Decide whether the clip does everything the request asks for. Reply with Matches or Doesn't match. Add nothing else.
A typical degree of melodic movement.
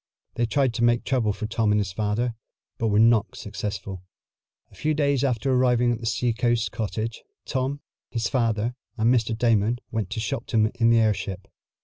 Doesn't match